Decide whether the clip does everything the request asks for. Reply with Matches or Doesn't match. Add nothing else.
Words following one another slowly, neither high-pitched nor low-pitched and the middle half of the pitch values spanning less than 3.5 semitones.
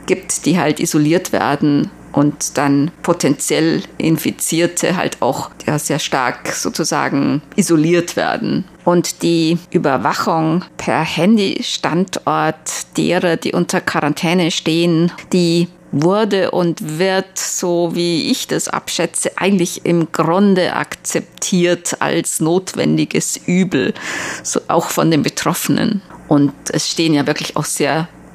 Matches